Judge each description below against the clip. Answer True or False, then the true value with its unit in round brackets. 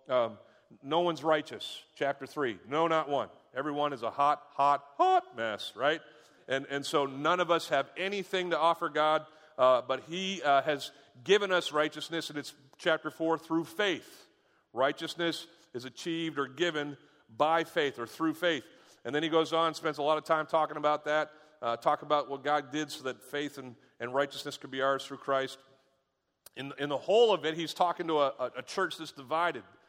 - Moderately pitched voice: True (150 Hz)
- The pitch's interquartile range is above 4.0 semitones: False (3.0 semitones)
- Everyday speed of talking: True (195 wpm)